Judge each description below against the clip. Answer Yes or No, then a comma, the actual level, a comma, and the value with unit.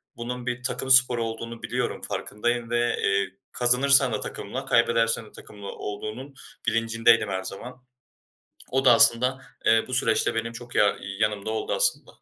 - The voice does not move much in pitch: Yes, narrow, 2.0 semitones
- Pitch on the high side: No, low, 115 Hz